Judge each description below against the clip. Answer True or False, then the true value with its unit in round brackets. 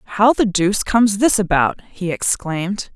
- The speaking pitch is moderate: False (200 Hz)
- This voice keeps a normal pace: True (160 wpm)